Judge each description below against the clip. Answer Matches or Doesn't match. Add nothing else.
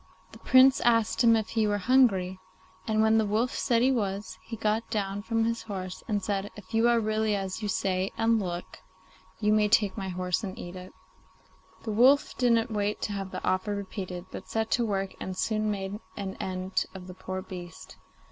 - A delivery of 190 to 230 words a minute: Matches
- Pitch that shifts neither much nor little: Matches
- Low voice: Doesn't match